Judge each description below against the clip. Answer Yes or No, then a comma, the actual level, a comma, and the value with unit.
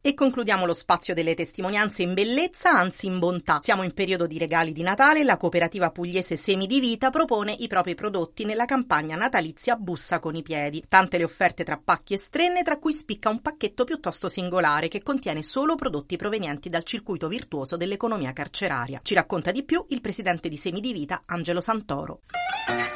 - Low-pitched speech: No, high, 190 Hz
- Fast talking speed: Yes, fast, 190 wpm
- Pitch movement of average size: No, wide, 5.8 semitones